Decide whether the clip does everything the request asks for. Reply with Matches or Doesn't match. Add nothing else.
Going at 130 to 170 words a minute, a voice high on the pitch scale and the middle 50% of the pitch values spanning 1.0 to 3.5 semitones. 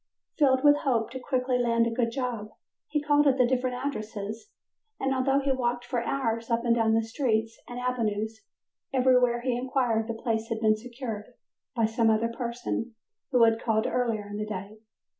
Doesn't match